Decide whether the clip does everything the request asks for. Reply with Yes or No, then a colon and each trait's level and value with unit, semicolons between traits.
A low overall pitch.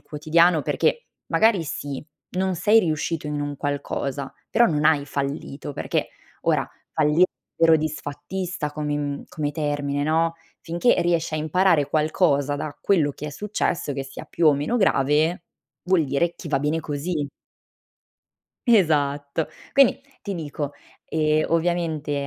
No: medium, 155 Hz